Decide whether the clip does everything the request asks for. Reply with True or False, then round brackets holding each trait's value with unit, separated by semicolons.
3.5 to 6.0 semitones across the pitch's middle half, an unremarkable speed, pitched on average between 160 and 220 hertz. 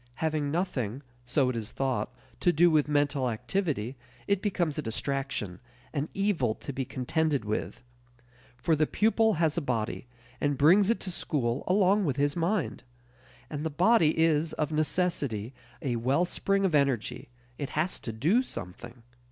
False (5.3 semitones; 160 wpm; 150 Hz)